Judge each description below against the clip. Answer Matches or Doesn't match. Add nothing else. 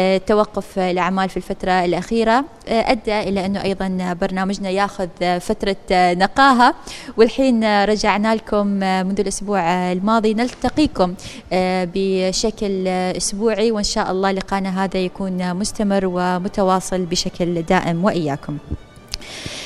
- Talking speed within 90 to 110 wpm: Matches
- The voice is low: Doesn't match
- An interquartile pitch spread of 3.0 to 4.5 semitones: Doesn't match